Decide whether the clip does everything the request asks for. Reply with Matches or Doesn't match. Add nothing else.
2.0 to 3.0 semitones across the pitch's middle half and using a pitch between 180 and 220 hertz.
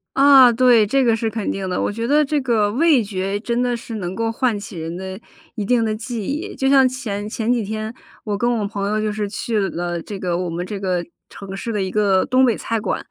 Doesn't match